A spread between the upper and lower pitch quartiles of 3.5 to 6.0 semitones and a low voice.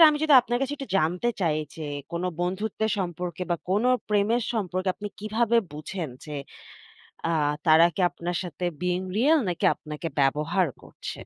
No: average, 4.4 semitones; medium, 185 Hz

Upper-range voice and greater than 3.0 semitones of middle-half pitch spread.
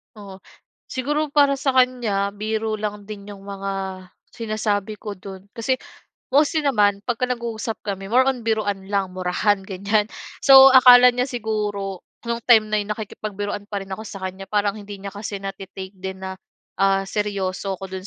No: high, 205 Hz; average, 2.7 semitones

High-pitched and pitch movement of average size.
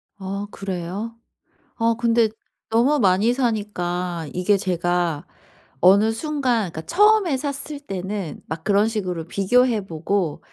Yes: high, 200 Hz; average, 4.7 semitones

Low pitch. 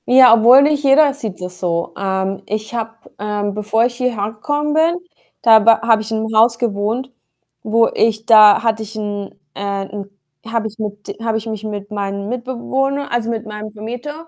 No: high, 220 Hz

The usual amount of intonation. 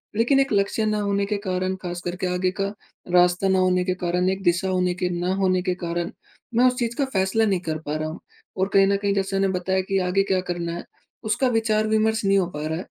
No: narrow, 2.1 semitones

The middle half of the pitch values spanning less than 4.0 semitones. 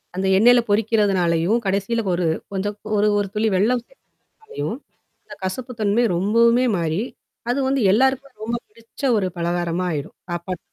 No: average, 4.4 semitones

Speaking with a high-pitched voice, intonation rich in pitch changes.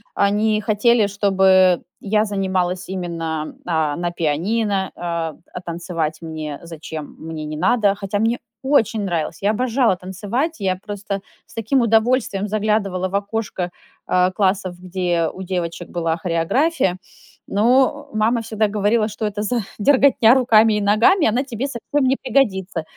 No: high, 200 Hz; average, 4.0 semitones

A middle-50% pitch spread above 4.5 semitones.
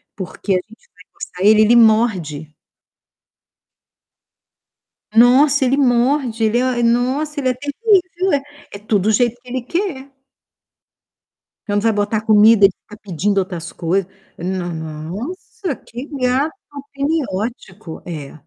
Yes: average, 5.3 semitones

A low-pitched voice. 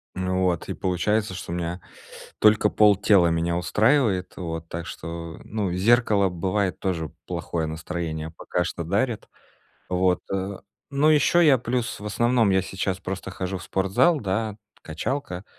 Yes: very low, 95 Hz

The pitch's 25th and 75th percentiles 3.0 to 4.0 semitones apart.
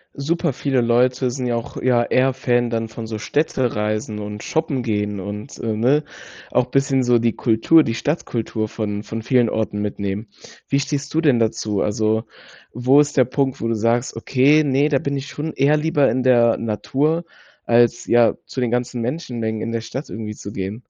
Yes: average, 3.7 semitones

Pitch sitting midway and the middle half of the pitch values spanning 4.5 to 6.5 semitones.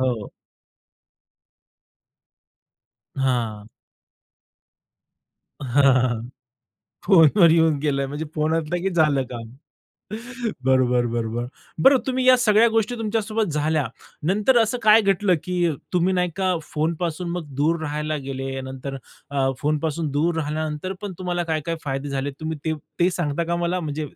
Yes: medium, 155 Hz; average, 4.8 semitones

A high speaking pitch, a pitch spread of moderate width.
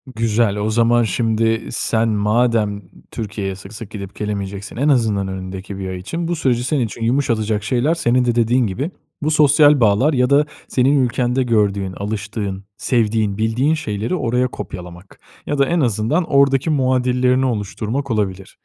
No: low, 115 Hz; average, 3.8 semitones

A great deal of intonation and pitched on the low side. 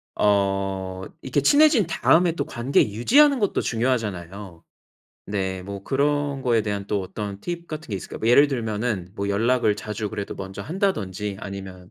Yes: wide, 6.2 semitones; low, 105 Hz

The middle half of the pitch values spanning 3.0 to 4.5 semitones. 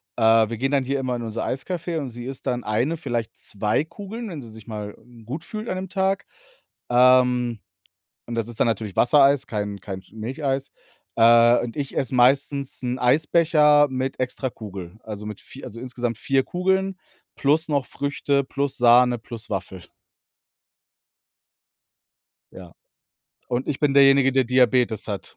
Yes: average, 3.8 semitones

